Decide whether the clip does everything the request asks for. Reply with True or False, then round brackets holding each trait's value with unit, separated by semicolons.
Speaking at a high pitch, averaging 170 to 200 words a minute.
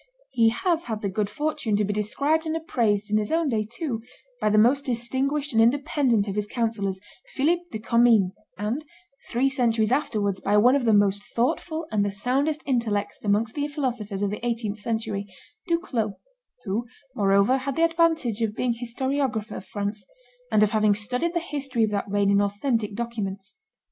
True (230 Hz; 180 wpm)